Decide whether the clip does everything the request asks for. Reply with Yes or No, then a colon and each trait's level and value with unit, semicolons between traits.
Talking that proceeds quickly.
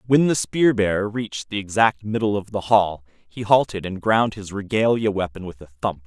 Yes: fast, 210 wpm